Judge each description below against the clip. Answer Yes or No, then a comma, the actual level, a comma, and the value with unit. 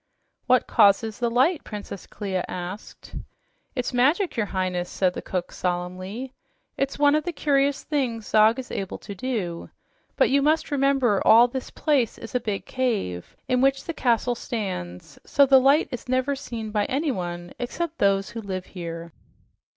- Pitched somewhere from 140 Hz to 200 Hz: No, high, 235 Hz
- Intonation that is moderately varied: No, wide, 5.9 semitones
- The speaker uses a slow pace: No, average, 165 wpm